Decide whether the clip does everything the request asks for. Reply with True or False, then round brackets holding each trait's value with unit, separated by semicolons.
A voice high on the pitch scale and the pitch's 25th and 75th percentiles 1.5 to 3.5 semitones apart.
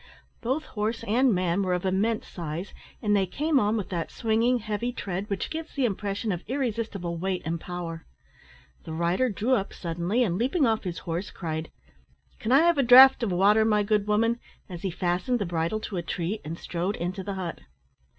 False (200 Hz; 4.5 semitones)